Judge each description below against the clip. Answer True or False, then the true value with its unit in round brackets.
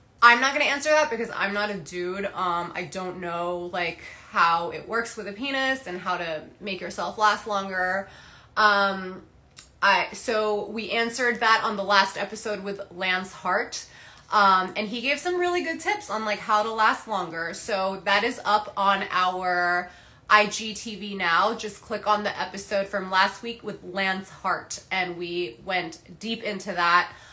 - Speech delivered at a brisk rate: False (175 wpm)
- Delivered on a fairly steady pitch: False (3.0 semitones)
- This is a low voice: False (200 Hz)